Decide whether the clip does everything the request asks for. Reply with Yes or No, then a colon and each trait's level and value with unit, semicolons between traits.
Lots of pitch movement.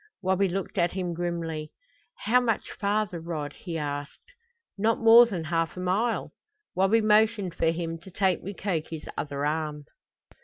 No: average, 4.0 semitones